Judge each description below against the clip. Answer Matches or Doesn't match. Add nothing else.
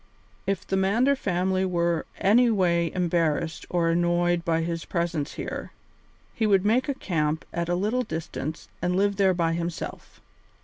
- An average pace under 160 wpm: Matches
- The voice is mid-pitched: Matches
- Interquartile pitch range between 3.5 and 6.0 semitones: Doesn't match